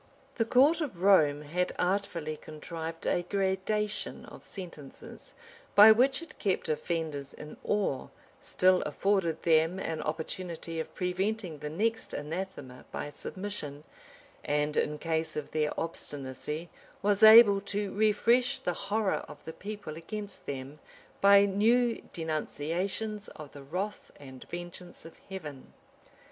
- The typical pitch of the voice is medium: Yes, medium, 180 Hz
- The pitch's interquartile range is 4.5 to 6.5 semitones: Yes, average, 4.9 semitones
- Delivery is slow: Yes, slow, 130 wpm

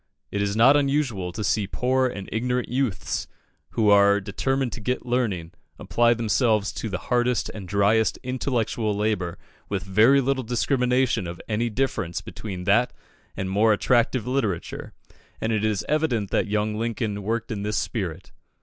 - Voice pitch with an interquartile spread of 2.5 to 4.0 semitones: Yes, average, 3.5 semitones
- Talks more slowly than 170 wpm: Yes, average, 160 wpm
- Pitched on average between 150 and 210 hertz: No, low, 110 Hz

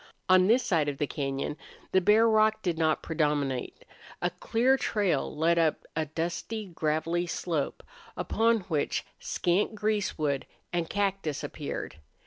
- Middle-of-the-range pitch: Yes, medium, 170 Hz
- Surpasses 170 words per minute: No, slow, 135 wpm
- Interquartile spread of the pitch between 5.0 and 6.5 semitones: Yes, average, 5.3 semitones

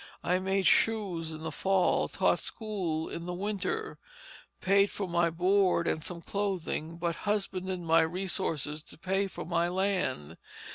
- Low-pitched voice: No, medium, 180 Hz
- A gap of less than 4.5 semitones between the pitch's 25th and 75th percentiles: Yes, average, 2.9 semitones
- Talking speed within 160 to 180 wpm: No, average, 150 wpm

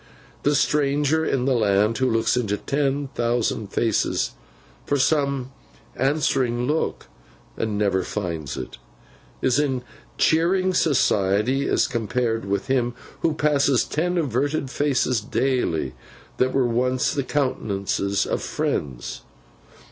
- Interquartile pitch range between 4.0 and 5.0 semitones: Yes, average, 4.5 semitones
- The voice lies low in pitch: Yes, low, 130 Hz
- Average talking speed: No, slow, 120 wpm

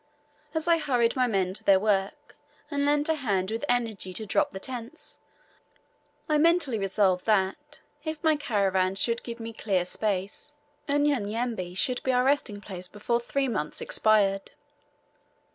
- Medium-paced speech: Yes, average, 160 wpm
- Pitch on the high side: Yes, high, 225 Hz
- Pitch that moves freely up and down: Yes, wide, 6.2 semitones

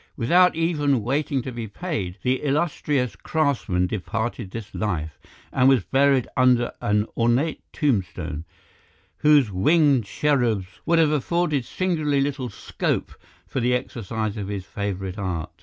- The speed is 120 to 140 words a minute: Yes, slow, 135 wpm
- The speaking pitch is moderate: No, low, 125 Hz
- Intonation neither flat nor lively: No, wide, 6.1 semitones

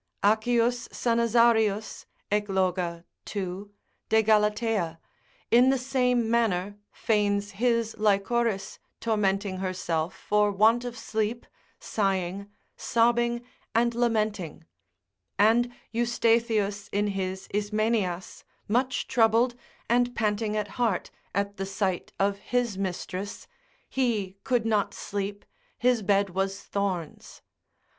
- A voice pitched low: No, high, 210 Hz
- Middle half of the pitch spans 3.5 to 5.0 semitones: No, average, 3.0 semitones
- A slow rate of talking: Yes, slow, 105 wpm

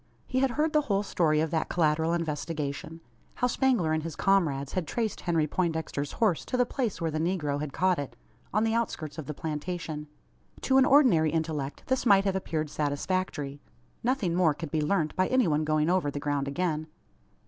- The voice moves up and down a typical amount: Yes, average, 4.4 semitones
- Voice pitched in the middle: Yes, medium, 165 Hz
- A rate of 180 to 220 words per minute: Yes, average, 195 wpm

